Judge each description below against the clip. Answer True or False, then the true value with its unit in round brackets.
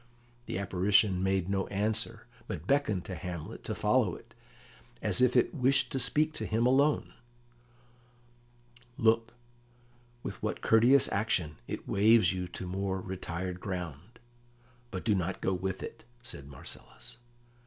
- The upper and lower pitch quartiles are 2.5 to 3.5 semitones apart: False (4.2 semitones)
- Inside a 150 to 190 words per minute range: False (140 wpm)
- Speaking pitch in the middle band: False (95 Hz)